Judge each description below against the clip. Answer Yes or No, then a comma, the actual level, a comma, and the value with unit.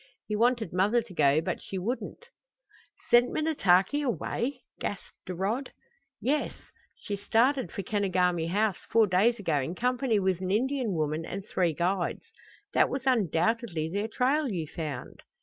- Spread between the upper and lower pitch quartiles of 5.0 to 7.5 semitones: Yes, average, 5.3 semitones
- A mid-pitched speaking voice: No, high, 205 Hz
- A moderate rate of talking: Yes, average, 150 wpm